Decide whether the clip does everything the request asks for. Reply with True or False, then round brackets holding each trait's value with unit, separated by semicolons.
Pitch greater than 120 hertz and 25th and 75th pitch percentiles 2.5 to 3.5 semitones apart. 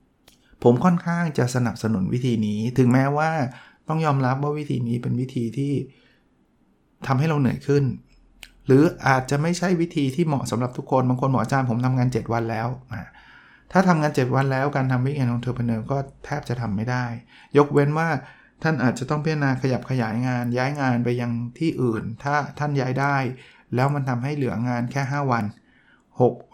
True (130 Hz; 3.0 semitones)